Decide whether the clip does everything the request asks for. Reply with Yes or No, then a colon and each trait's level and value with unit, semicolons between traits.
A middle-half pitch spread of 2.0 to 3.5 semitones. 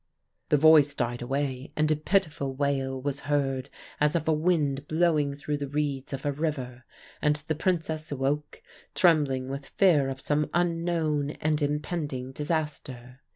Yes: narrow, 2.4 semitones